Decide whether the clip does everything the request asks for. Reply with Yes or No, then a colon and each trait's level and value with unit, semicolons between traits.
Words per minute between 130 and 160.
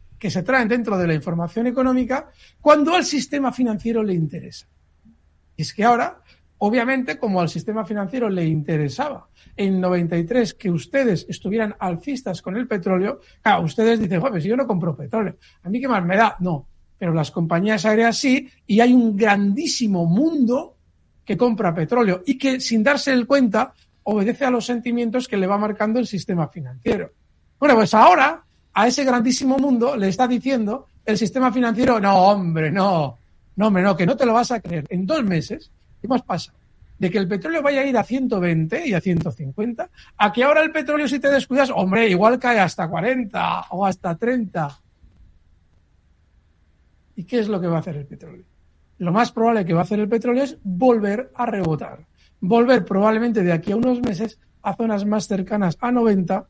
No: average, 185 wpm